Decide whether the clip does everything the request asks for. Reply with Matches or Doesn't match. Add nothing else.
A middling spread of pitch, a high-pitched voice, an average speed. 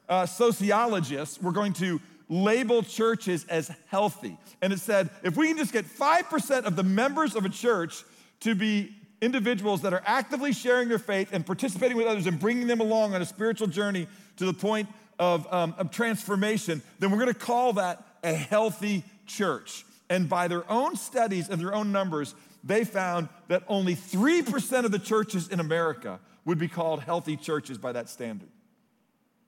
Matches